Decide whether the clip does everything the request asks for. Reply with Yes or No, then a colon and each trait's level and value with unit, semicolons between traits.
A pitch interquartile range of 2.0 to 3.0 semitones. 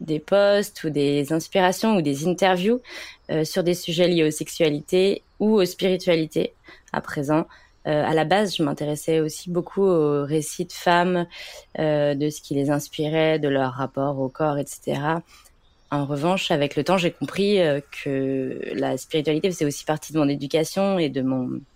No: average, 3.7 semitones